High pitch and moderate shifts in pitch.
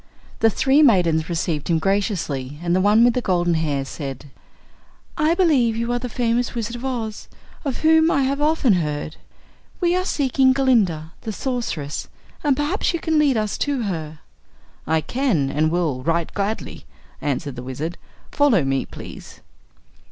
No: high, 210 Hz; wide, 8.9 semitones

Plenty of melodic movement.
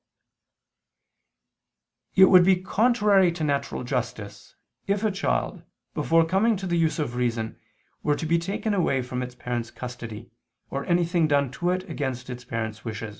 Yes: wide, 6.9 semitones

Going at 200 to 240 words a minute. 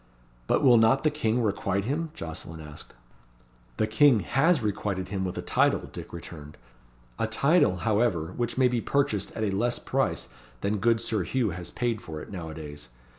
No: average, 185 wpm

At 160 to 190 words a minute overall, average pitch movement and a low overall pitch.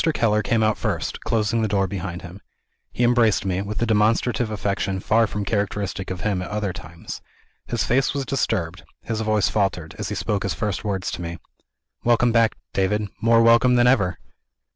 Yes: average, 185 wpm; average, 3.0 semitones; low, 105 Hz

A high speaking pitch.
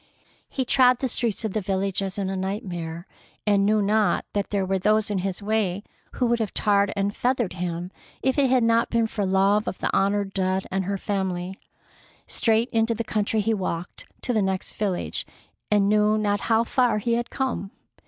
Yes: high, 205 Hz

